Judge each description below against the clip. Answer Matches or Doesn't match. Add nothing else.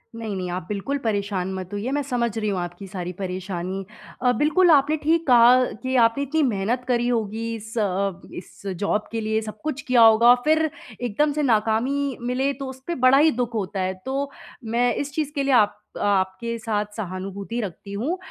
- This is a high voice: Matches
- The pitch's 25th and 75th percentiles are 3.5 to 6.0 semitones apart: Matches